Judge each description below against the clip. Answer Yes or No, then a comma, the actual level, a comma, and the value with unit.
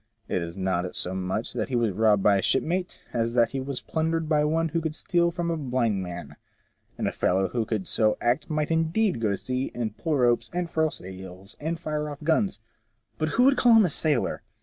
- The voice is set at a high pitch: No, low, 130 Hz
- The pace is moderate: No, fast, 230 wpm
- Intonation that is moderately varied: No, wide, 7.5 semitones